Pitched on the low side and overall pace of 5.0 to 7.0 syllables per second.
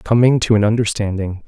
Yes: low, 110 Hz; 5.6 syllables/s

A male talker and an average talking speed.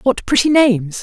No: female; average, 175 wpm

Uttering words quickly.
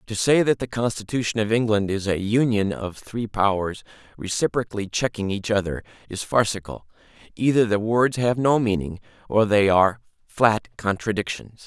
No: average, 155 wpm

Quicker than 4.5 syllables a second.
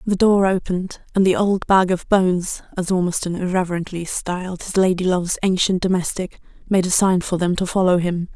Yes: 5.5 syllables/s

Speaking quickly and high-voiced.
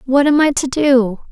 Yes: fast, 230 wpm; very high, 270 Hz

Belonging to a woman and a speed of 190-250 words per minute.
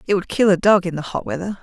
No: female; fast, 330 wpm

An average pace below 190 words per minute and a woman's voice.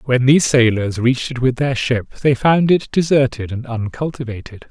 No: average, 180 wpm; male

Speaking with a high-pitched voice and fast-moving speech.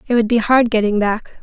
Yes: high, 225 Hz; fast, 250 wpm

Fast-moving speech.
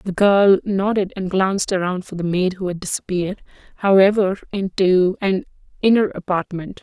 No: average, 150 wpm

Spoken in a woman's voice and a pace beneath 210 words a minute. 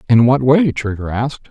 No: male; average, 200 wpm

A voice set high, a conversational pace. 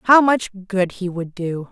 No: high, 200 Hz; fast, 210 wpm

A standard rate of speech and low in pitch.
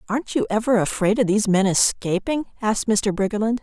No: average, 180 wpm; high, 215 Hz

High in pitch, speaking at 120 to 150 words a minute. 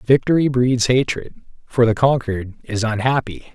No: low, 120 Hz; slow, 135 wpm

